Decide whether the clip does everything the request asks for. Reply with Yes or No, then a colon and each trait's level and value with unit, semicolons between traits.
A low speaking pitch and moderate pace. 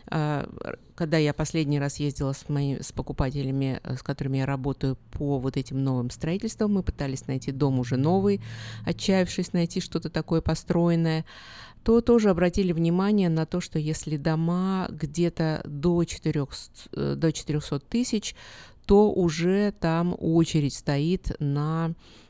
No: medium, 160 Hz; average, 130 wpm